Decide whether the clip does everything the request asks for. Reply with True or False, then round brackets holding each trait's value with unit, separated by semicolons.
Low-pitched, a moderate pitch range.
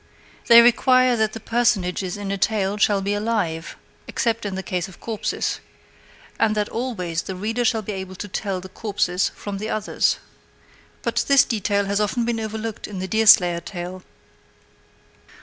False (205 Hz; 3.0 semitones)